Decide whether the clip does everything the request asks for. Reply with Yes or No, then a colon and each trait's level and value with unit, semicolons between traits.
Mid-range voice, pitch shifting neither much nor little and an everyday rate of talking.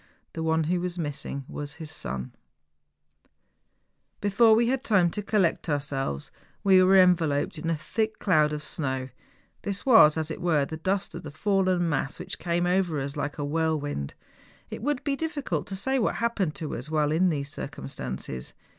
Yes: medium, 165 Hz; average, 4.7 semitones; average, 180 wpm